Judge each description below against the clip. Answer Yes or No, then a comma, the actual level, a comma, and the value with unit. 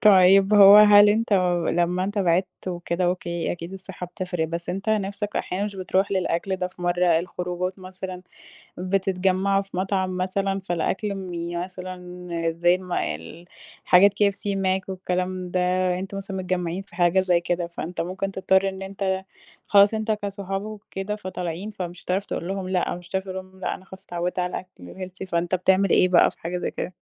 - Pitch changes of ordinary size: No, narrow, 1.6 semitones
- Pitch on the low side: No, medium, 185 Hz